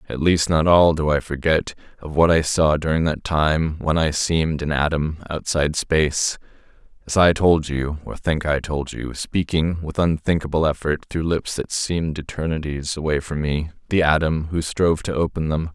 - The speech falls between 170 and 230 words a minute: Yes, average, 185 wpm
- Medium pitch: No, very low, 80 Hz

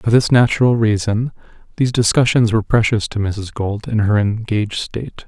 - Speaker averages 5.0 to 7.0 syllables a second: Yes, 5.5 syllables/s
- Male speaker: Yes, male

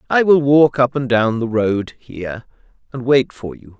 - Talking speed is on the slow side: No, fast, 205 wpm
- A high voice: No, low, 125 Hz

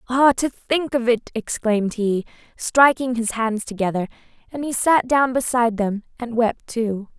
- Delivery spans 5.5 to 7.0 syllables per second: No, 4.5 syllables/s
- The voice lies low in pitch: No, high, 235 Hz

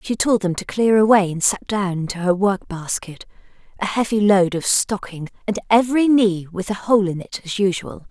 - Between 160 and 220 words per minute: Yes, fast, 205 wpm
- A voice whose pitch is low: No, high, 200 Hz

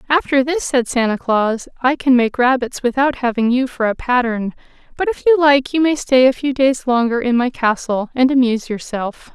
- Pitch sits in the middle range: No, very high, 255 Hz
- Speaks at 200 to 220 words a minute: Yes, fast, 205 wpm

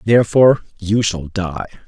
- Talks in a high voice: No, low, 100 Hz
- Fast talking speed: No, slow, 130 wpm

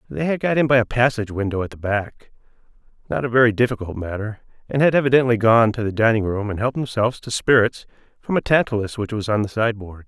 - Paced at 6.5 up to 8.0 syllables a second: Yes, 6.6 syllables/s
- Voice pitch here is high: No, low, 115 Hz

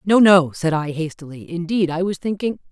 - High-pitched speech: No, medium, 175 Hz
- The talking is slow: No, average, 200 wpm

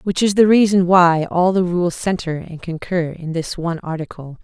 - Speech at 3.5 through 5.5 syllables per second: Yes, 4.9 syllables/s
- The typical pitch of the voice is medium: Yes, medium, 175 Hz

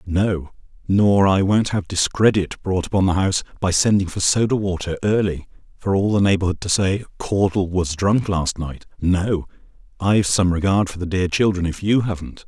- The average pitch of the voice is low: Yes, very low, 95 Hz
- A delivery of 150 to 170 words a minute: No, average, 185 wpm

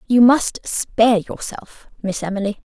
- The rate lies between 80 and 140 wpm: Yes, slow, 135 wpm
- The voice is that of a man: No, female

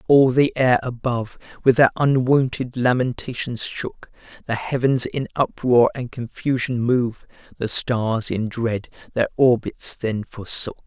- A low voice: Yes, low, 120 Hz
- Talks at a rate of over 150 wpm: No, slow, 135 wpm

